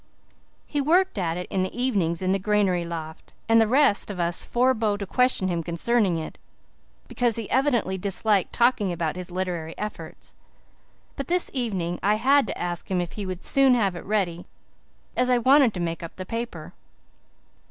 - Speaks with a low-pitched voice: No, high, 200 Hz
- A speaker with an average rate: Yes, average, 185 wpm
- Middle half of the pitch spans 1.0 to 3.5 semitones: No, wide, 5.5 semitones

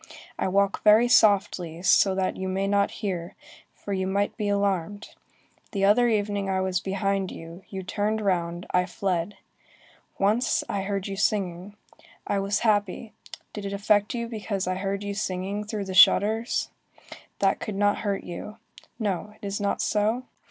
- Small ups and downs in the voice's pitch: Yes, narrow, 1.7 semitones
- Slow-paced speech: No, average, 165 wpm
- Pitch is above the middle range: Yes, high, 200 Hz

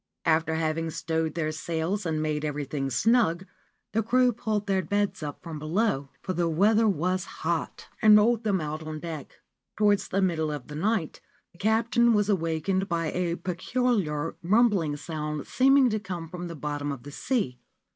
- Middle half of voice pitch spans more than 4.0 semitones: Yes, average, 5.2 semitones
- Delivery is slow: No, average, 175 wpm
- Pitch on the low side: No, medium, 170 Hz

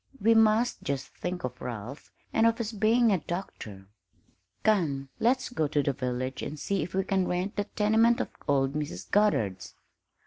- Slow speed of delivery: No, average, 175 wpm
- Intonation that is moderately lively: No, wide, 8.0 semitones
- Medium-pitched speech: Yes, medium, 180 Hz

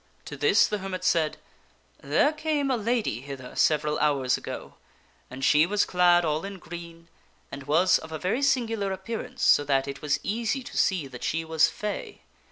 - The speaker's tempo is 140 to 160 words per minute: No, average, 185 wpm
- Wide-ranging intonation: Yes, wide, 6.0 semitones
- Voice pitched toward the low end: No, medium, 170 Hz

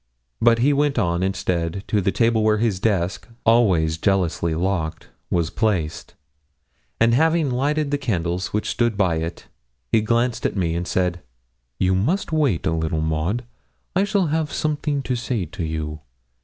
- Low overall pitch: Yes, low, 100 Hz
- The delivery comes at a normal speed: Yes, average, 165 wpm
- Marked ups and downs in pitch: Yes, wide, 6.5 semitones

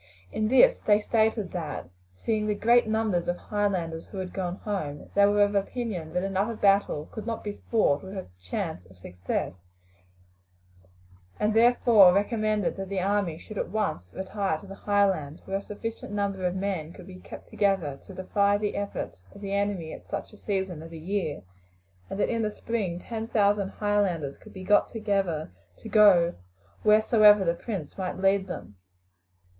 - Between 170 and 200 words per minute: Yes, average, 180 wpm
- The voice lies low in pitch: No, high, 200 Hz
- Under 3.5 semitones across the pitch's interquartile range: Yes, average, 3.0 semitones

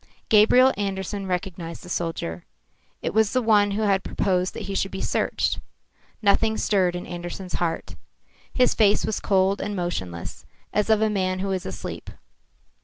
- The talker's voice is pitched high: Yes, high, 195 Hz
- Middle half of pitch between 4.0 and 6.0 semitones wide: No, average, 2.7 semitones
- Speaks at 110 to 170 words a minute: Yes, average, 165 wpm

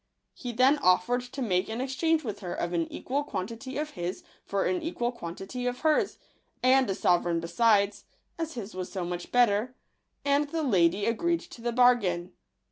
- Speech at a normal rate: Yes, average, 180 wpm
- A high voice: Yes, high, 235 Hz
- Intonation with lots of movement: Yes, wide, 6.2 semitones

